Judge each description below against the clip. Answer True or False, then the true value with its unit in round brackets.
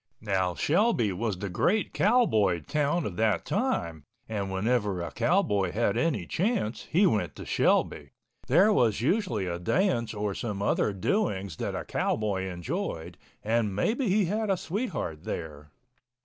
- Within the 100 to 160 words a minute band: True (150 wpm)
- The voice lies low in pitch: True (110 Hz)